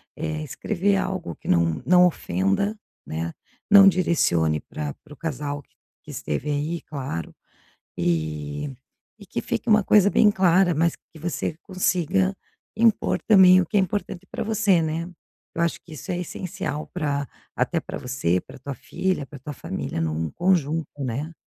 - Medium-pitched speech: Yes, medium, 160 Hz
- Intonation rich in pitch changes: Yes, wide, 6.2 semitones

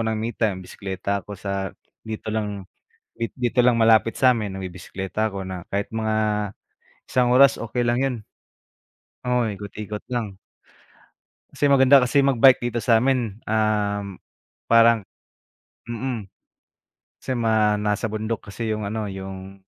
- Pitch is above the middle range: No, low, 110 Hz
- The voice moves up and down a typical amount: Yes, average, 3.1 semitones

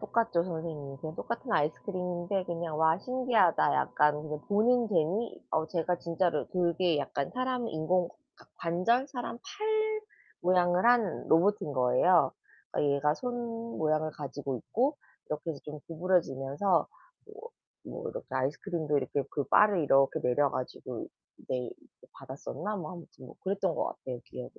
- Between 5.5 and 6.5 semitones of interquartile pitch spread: Yes, wide, 5.8 semitones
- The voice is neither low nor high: Yes, medium, 170 Hz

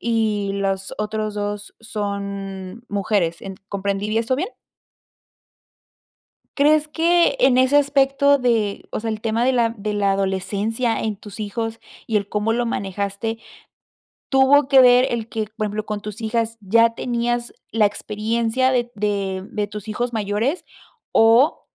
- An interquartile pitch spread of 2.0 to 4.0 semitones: Yes, average, 2.8 semitones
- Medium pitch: No, high, 220 Hz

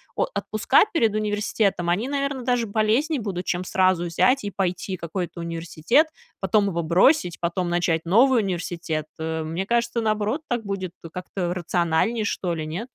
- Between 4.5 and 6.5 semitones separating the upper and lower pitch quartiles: Yes, average, 4.8 semitones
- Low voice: No, high, 190 Hz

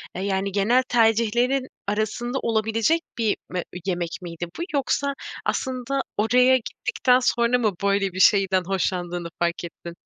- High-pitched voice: Yes, high, 215 Hz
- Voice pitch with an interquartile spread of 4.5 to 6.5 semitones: Yes, average, 4.9 semitones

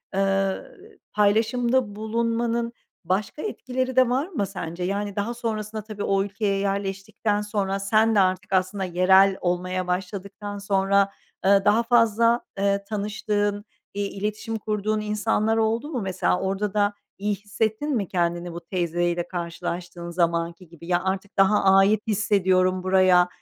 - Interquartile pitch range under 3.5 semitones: Yes, narrow, 2.4 semitones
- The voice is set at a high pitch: Yes, high, 200 Hz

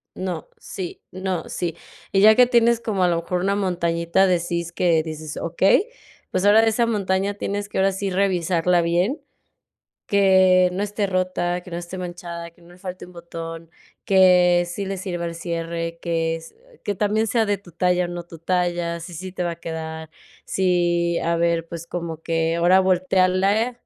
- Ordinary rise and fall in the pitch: No, narrow, 2.2 semitones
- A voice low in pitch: No, medium, 180 Hz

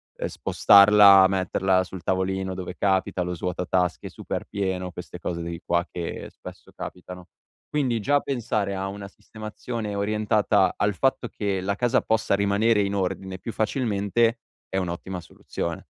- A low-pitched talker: Yes, very low, 95 Hz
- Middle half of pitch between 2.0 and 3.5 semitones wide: Yes, narrow, 2.4 semitones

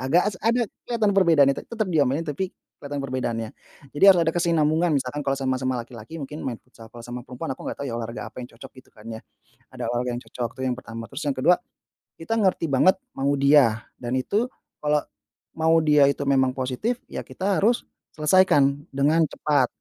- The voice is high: No, medium, 140 Hz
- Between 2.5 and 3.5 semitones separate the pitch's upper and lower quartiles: No, average, 4.6 semitones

